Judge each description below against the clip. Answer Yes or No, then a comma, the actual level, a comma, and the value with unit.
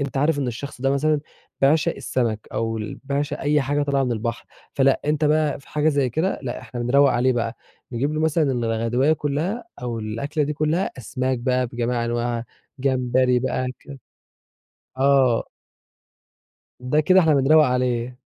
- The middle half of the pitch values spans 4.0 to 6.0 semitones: No, average, 3.3 semitones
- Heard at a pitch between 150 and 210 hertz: No, low, 135 Hz